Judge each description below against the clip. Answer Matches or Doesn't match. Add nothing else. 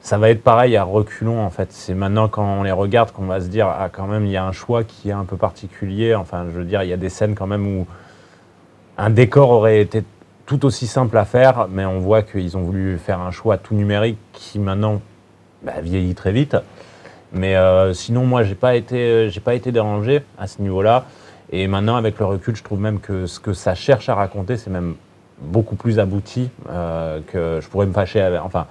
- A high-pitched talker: Doesn't match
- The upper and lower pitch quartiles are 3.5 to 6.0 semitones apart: Doesn't match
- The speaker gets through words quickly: Matches